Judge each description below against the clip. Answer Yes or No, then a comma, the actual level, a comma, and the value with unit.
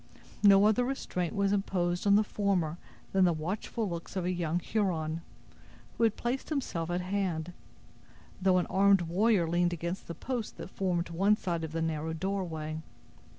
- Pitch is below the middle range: No, medium, 180 Hz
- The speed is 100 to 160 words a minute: No, average, 170 wpm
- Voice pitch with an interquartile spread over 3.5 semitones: No, average, 3.0 semitones